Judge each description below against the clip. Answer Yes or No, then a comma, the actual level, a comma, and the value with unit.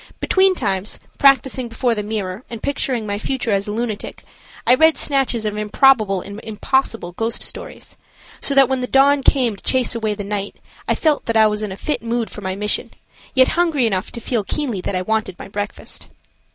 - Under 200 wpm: No, fast, 205 wpm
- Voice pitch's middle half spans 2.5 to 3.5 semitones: No, average, 4.3 semitones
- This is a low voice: No, high, 225 Hz